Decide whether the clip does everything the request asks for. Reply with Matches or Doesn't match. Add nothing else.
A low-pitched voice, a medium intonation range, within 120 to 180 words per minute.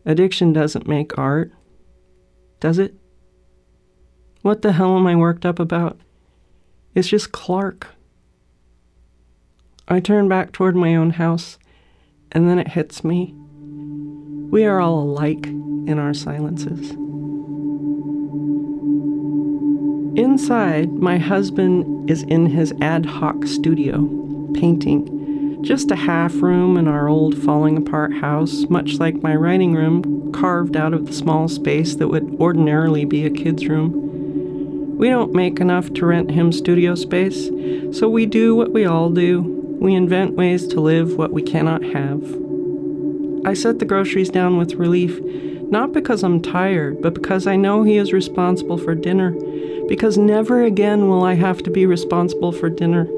Doesn't match